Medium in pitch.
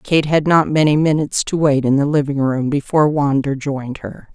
Yes: medium, 145 Hz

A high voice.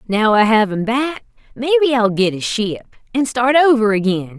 Yes: high, 230 Hz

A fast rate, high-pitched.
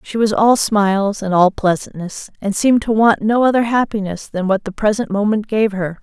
Yes: fast, 210 wpm; high, 210 Hz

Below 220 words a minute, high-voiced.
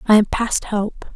Yes: fast, 205 wpm; high, 210 Hz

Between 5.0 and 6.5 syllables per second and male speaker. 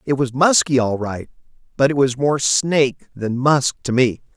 No: 4.5 syllables/s; male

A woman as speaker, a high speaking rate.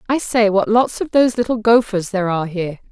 Yes: female; fast, 225 wpm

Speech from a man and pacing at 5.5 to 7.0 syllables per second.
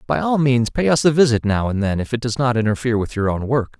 Yes: male; 6.3 syllables/s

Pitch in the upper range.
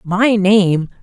Yes: high, 195 Hz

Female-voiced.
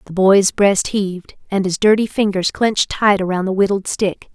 Yes: female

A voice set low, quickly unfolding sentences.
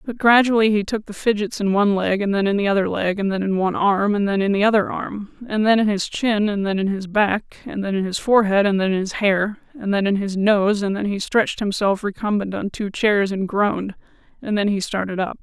No: high, 205 Hz; fast, 260 wpm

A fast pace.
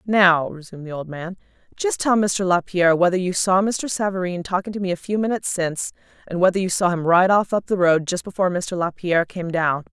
Yes: fast, 225 wpm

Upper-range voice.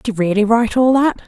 Yes: high, 230 Hz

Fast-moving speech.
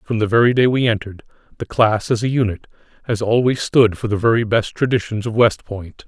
Yes: fast, 215 wpm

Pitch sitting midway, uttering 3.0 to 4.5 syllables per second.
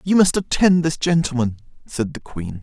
No: medium, 145 Hz; 4.9 syllables/s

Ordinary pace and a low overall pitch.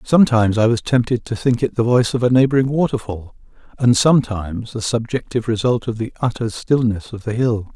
Yes: average, 195 wpm; low, 115 Hz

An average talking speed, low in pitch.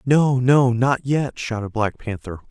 Yes: average, 170 wpm; low, 125 Hz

